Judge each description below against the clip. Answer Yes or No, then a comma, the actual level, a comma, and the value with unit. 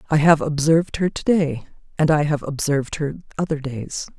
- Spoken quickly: No, average, 185 wpm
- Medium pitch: Yes, medium, 150 Hz